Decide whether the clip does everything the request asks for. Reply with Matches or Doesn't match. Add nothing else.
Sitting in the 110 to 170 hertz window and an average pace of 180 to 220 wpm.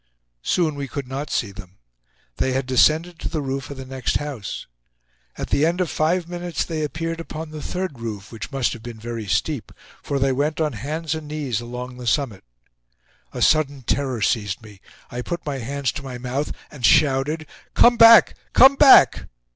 Matches